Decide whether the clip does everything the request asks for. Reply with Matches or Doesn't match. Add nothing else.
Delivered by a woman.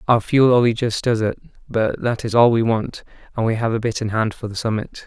Doesn't match